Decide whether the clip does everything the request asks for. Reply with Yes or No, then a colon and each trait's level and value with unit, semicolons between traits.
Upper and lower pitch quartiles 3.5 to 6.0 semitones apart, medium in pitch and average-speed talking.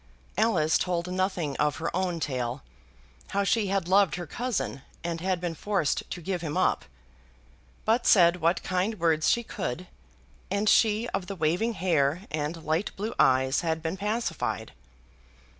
Yes: average, 4.0 semitones; medium, 175 Hz; average, 160 wpm